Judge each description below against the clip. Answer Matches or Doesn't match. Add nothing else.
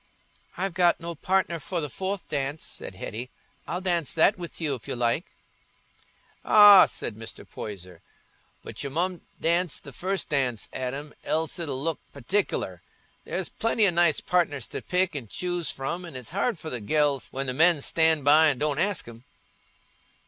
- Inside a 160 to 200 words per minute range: Matches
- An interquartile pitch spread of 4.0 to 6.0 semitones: Matches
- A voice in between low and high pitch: Matches